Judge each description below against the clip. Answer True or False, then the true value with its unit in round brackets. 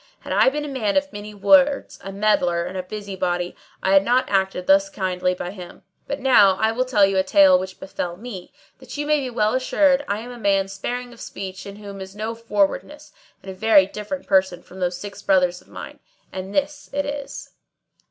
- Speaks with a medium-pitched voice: False (200 Hz)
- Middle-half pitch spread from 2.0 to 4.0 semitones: False (4.7 semitones)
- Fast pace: True (215 wpm)